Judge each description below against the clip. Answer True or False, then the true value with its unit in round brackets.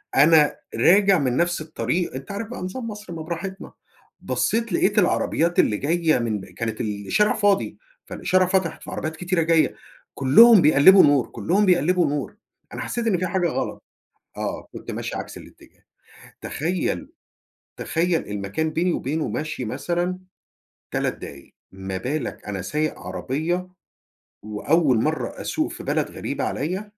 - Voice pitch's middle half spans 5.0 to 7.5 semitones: True (5.4 semitones)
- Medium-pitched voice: True (165 Hz)